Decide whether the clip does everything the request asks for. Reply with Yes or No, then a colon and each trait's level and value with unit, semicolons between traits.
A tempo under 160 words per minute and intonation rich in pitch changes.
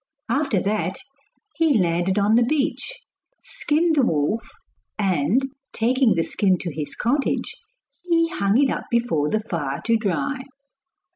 Yes: average, 140 wpm; wide, 7.5 semitones